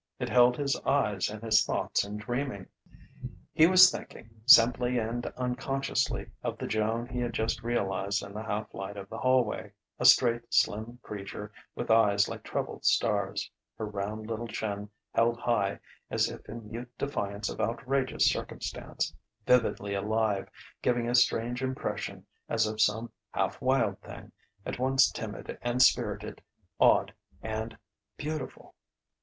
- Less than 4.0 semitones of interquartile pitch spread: Yes, average, 2.8 semitones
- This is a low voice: Yes, low, 115 Hz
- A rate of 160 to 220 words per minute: No, average, 150 wpm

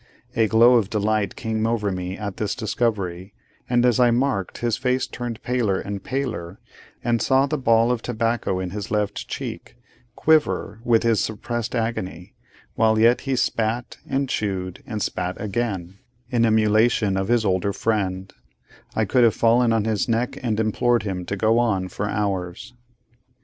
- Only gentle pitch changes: No, average, 3.2 semitones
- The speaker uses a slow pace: No, average, 165 wpm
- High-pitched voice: No, low, 110 Hz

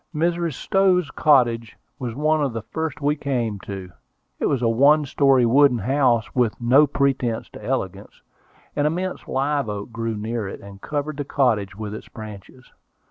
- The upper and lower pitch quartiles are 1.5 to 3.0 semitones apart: No, average, 4.4 semitones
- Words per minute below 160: No, average, 170 wpm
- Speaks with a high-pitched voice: No, low, 130 Hz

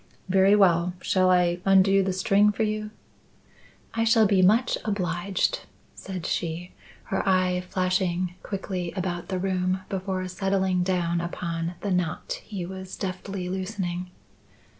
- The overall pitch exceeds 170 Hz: Yes, medium, 185 Hz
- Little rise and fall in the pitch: Yes, narrow, 1.5 semitones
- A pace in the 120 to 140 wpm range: Yes, slow, 135 wpm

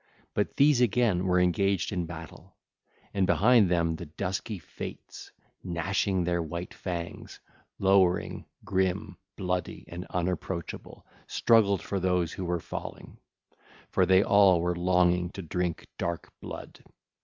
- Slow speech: Yes, slow, 130 wpm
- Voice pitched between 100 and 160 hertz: No, very low, 90 Hz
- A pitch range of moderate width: No, narrow, 2.0 semitones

